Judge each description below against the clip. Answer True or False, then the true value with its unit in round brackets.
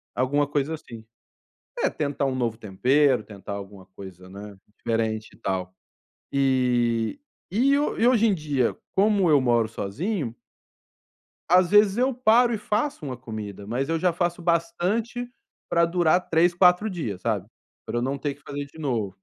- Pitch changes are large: True (7.9 semitones)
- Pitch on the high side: False (140 Hz)